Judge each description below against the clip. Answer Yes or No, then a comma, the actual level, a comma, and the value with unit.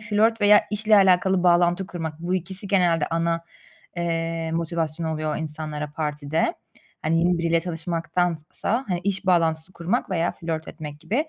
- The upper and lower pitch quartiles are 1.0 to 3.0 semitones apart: Yes, narrow, 2.5 semitones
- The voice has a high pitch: No, medium, 170 Hz